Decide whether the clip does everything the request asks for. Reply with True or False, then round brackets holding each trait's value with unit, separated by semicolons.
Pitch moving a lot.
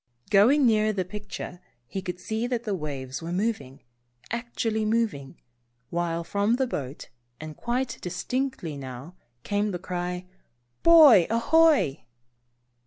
True (5.7 semitones)